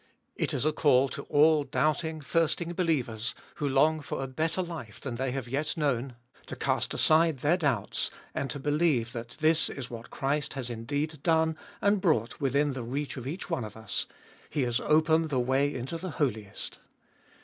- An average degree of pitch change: Yes, average, 4.0 semitones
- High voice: No, medium, 145 Hz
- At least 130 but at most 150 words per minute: No, average, 185 wpm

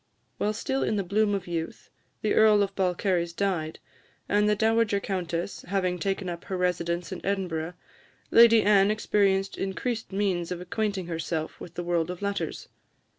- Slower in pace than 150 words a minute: No, average, 165 wpm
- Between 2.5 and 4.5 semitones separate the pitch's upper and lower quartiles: Yes, average, 2.8 semitones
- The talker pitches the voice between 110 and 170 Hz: No, high, 190 Hz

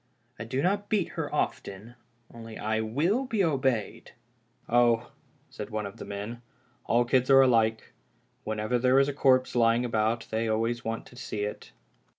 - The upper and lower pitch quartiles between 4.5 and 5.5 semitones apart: No, average, 2.9 semitones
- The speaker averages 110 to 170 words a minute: No, average, 180 wpm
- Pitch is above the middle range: No, low, 120 Hz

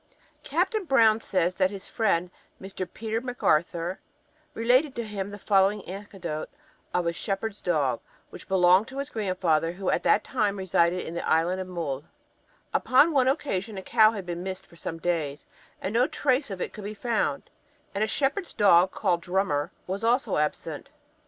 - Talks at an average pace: Yes, average, 175 wpm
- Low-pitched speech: No, high, 195 Hz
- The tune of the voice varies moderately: Yes, average, 4.2 semitones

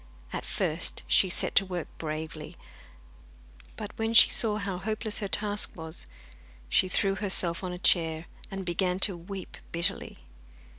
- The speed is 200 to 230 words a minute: No, average, 150 wpm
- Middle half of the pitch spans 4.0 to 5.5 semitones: No, average, 3.3 semitones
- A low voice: No, medium, 185 Hz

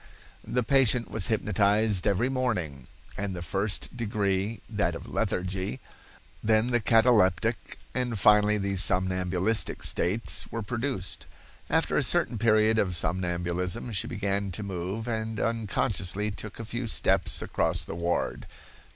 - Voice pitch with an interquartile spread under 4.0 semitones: Yes, average, 3.3 semitones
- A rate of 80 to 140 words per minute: Yes, slow, 135 wpm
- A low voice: Yes, low, 105 Hz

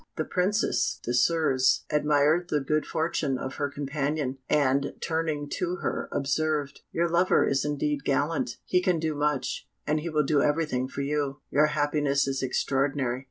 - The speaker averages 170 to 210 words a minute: No, average, 160 wpm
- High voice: No, medium, 145 Hz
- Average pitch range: No, narrow, 2.3 semitones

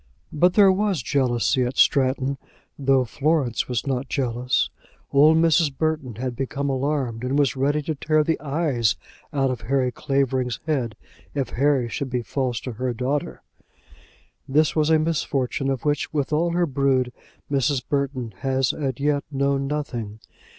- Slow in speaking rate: No, average, 155 wpm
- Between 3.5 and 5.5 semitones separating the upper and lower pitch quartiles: No, average, 2.8 semitones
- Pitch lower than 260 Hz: Yes, low, 135 Hz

